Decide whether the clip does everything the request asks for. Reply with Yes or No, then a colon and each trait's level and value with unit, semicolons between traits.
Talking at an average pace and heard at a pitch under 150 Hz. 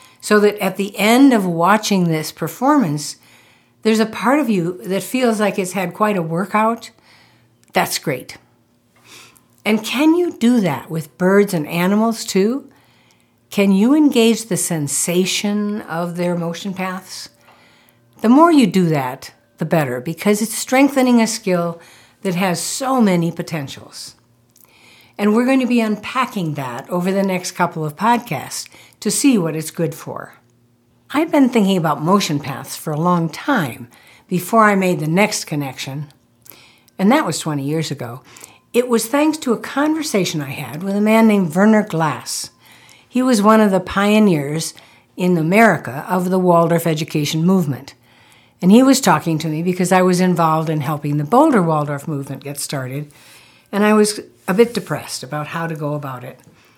No: average, 165 wpm; medium, 180 Hz